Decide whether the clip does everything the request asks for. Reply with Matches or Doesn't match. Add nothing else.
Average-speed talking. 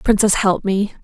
Matches